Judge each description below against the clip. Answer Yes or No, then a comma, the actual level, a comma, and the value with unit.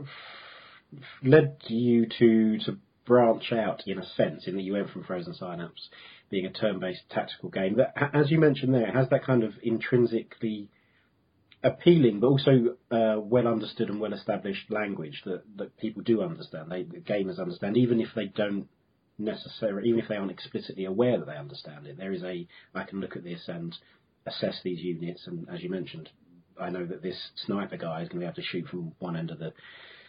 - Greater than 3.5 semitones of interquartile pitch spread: Yes, average, 4.5 semitones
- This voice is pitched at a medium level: No, low, 110 Hz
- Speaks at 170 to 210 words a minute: Yes, average, 195 wpm